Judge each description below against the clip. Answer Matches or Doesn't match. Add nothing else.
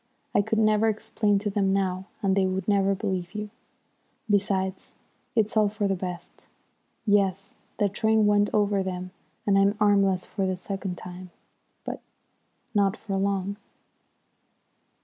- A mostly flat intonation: Matches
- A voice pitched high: Matches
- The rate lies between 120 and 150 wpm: Matches